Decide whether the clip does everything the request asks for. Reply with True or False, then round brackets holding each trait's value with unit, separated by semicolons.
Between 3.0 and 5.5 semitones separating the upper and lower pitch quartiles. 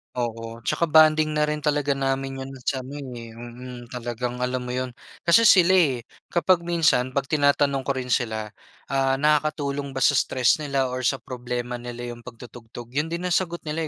True (3.6 semitones)